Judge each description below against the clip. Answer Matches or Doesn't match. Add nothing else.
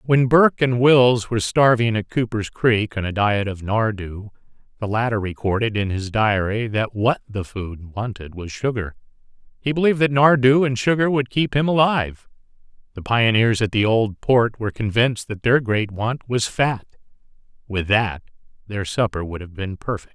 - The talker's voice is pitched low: Matches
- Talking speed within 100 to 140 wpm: Doesn't match